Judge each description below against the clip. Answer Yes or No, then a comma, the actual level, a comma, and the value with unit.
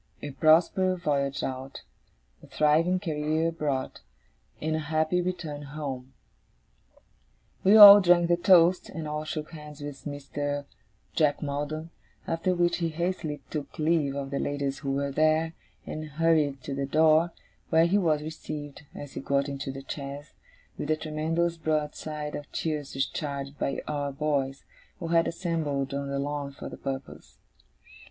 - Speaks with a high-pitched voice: No, medium, 150 Hz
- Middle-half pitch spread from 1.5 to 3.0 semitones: Yes, average, 2.7 semitones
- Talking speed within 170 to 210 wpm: No, average, 155 wpm